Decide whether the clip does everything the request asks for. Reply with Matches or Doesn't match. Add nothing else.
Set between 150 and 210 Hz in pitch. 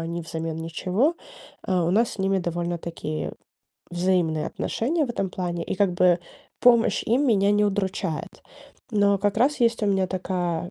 Matches